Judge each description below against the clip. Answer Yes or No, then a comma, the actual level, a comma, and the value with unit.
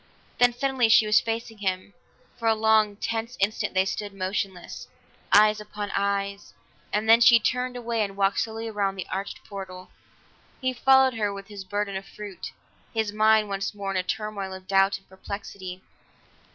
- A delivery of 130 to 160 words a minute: No, average, 180 wpm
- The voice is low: No, high, 205 Hz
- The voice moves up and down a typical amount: No, narrow, 2.2 semitones